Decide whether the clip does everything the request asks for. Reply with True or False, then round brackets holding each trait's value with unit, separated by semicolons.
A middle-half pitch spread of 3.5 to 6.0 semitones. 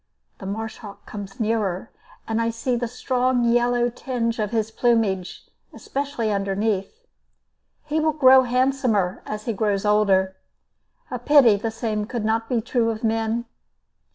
False (2.7 semitones)